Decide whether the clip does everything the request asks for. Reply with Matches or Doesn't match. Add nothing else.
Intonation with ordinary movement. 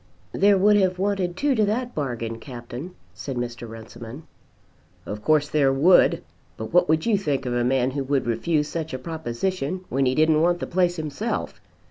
Doesn't match